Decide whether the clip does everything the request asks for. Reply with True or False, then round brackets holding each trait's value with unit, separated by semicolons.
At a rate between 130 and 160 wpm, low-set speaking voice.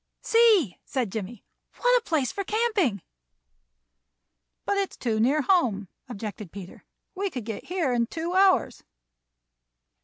False (140 wpm; 280 Hz)